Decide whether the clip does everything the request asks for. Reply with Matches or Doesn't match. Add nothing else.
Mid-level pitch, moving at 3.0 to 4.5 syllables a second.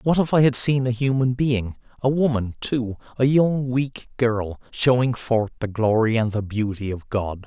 Doesn't match